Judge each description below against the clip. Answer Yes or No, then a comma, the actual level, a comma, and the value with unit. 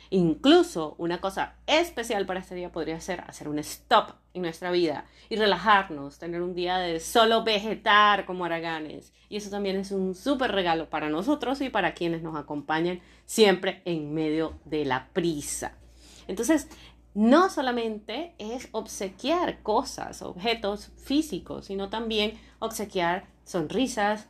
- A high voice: Yes, high, 195 Hz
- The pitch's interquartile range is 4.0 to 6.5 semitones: Yes, average, 4.9 semitones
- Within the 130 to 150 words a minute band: Yes, average, 140 wpm